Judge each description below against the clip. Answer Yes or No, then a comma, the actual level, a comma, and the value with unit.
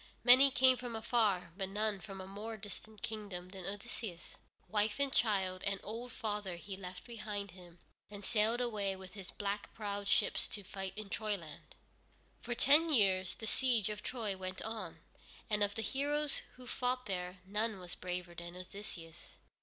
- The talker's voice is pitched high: Yes, high, 205 Hz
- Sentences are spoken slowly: No, average, 170 wpm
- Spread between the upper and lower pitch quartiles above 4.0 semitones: No, average, 3.1 semitones